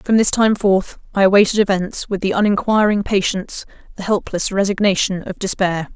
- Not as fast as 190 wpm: Yes, average, 160 wpm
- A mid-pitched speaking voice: No, high, 195 Hz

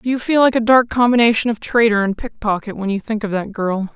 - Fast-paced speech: Yes, fast, 260 wpm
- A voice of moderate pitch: No, high, 225 Hz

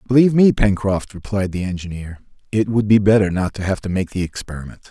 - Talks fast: Yes, fast, 210 wpm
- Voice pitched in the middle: No, low, 100 Hz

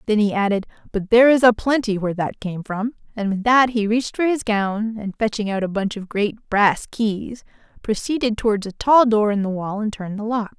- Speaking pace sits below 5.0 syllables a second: No, 5.4 syllables/s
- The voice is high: Yes, high, 215 Hz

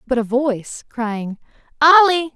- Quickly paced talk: No, slow, 125 wpm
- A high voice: Yes, very high, 265 Hz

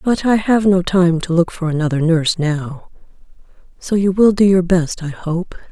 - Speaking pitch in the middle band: Yes, medium, 175 Hz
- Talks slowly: No, average, 200 wpm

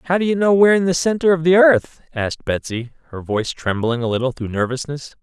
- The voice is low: No, medium, 150 Hz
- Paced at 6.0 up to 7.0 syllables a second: Yes, 6.1 syllables/s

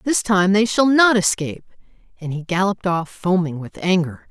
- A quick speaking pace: No, average, 180 wpm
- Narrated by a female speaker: Yes, female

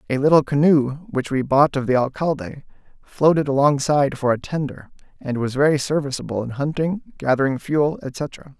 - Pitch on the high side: No, medium, 140 Hz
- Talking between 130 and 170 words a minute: Yes, average, 160 wpm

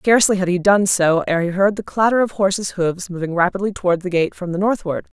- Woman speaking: Yes, female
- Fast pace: Yes, fast, 245 wpm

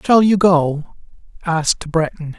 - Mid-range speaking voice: Yes, medium, 170 Hz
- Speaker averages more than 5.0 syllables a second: No, 4.0 syllables/s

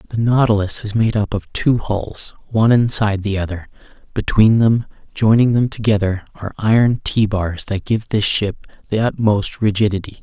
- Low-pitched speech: Yes, low, 105 Hz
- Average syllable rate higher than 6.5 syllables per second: No, 5.1 syllables/s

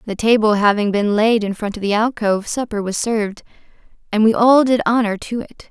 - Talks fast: Yes, fast, 210 wpm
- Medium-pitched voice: No, high, 215 Hz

